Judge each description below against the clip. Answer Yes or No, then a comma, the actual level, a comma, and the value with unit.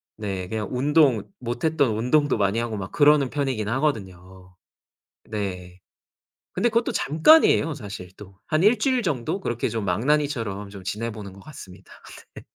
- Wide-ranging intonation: Yes, wide, 7.0 semitones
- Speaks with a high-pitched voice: No, low, 115 Hz